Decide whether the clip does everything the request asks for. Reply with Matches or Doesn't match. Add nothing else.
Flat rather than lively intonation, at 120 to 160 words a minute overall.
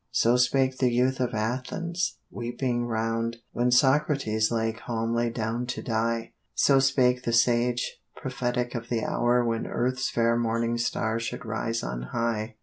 Matches